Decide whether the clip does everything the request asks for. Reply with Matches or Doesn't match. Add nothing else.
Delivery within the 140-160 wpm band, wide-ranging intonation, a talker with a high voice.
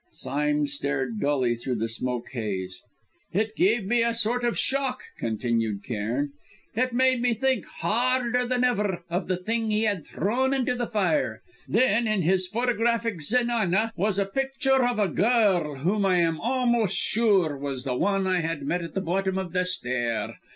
Doesn't match